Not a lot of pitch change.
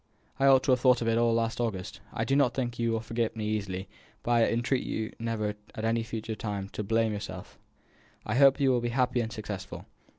Yes: narrow, 2.1 semitones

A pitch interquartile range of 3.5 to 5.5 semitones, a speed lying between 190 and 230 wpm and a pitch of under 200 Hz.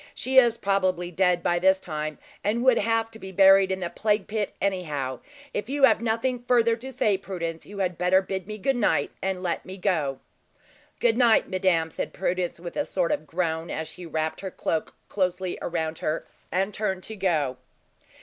Yes: average, 3.8 semitones; average, 195 wpm; high, 190 Hz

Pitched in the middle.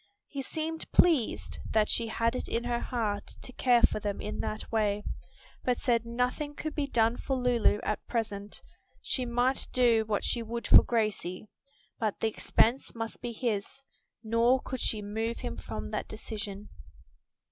No: high, 230 Hz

